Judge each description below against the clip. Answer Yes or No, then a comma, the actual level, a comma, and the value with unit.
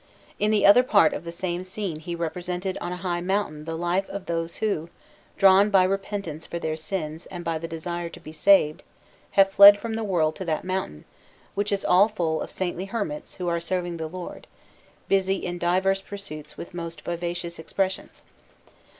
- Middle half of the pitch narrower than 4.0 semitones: Yes, average, 2.7 semitones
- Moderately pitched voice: Yes, medium, 180 Hz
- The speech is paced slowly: No, average, 190 wpm